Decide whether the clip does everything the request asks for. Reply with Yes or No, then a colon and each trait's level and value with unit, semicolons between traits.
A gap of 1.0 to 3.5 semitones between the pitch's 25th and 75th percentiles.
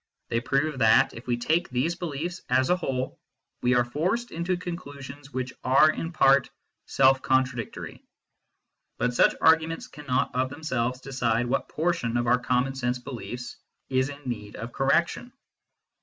No: average, 4.1 semitones